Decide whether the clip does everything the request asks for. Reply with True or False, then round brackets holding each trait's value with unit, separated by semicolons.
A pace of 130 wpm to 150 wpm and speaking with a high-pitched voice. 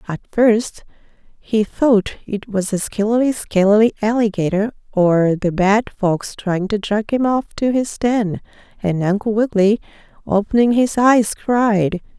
True (145 wpm; 215 Hz)